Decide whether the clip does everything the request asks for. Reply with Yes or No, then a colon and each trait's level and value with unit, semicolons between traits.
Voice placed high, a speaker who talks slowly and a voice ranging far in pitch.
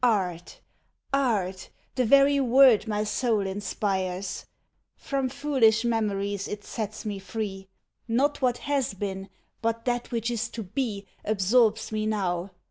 No: high, 220 Hz; slow, 130 wpm; average, 3.8 semitones